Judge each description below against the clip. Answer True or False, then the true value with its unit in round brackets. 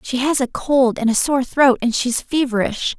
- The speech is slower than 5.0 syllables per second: True (4.6 syllables/s)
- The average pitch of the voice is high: True (255 Hz)